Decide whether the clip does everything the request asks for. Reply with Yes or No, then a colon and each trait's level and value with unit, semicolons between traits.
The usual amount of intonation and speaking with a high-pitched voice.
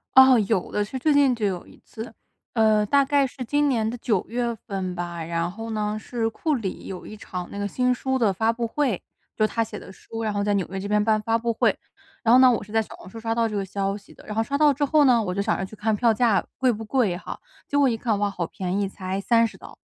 Yes: average, 3.5 semitones; high, 220 Hz